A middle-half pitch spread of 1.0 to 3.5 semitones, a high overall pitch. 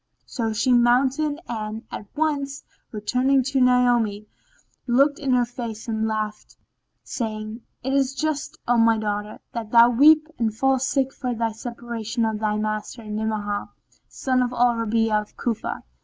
Yes: average, 3.2 semitones; high, 235 Hz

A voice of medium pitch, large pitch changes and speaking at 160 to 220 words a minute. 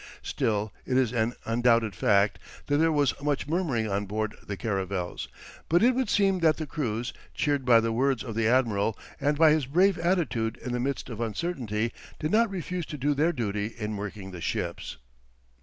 No: low, 125 Hz; wide, 6.2 semitones; average, 190 wpm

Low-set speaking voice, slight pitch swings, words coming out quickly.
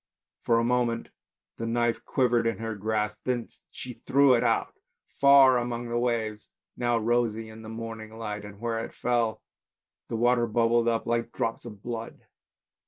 No: low, 115 Hz; narrow, 1.3 semitones; average, 170 wpm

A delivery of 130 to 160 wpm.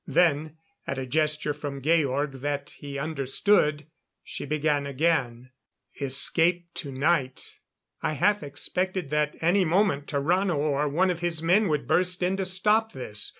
Yes: average, 150 wpm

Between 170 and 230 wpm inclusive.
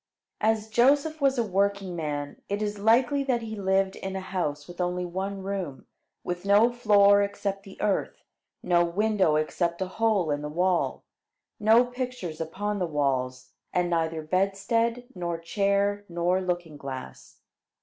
No: average, 155 wpm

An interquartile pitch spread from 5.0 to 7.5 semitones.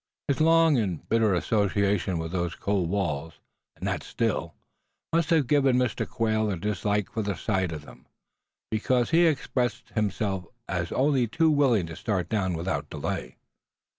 Yes: wide, 5.4 semitones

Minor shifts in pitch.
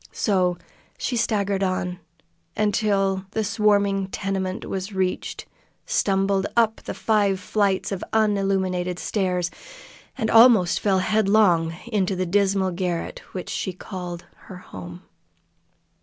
Yes: narrow, 2.1 semitones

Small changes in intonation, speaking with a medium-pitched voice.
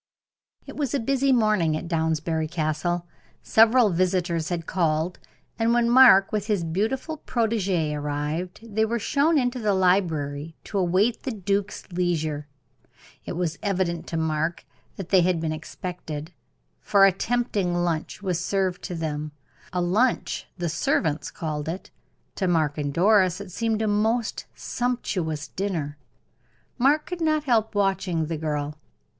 No: average, 5.2 semitones; medium, 180 Hz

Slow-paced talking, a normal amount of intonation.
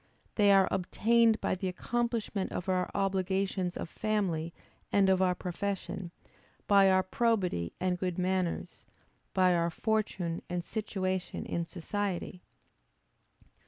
No: slow, 125 wpm; narrow, 2.2 semitones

